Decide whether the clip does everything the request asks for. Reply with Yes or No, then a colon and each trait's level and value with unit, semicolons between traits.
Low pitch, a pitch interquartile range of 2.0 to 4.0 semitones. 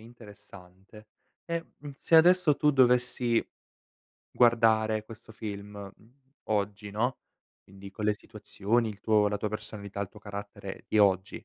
Yes: low, 110 Hz; average, 2.8 semitones